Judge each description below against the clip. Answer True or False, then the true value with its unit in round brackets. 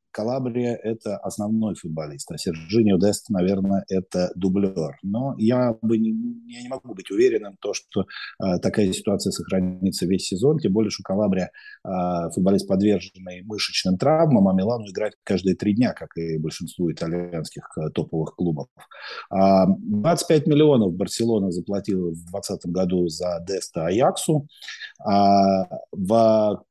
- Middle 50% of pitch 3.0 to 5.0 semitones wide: True (3.6 semitones)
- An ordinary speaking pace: True (140 wpm)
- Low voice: True (100 Hz)